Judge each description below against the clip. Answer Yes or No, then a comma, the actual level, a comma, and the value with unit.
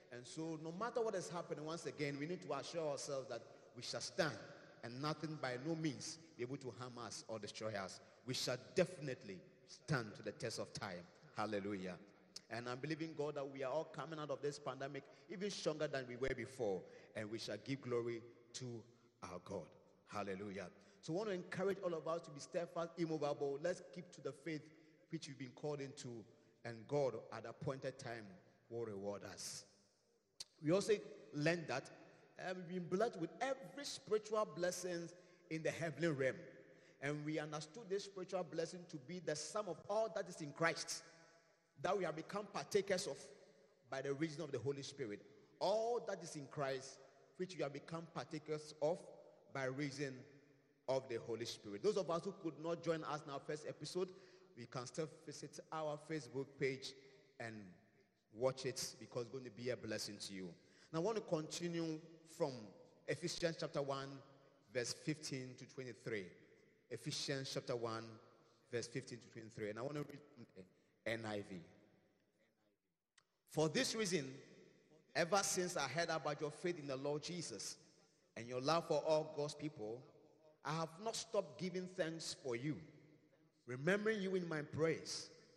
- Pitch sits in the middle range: Yes, medium, 150 Hz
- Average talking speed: Yes, average, 175 wpm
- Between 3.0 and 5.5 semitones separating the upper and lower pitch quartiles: Yes, average, 4.3 semitones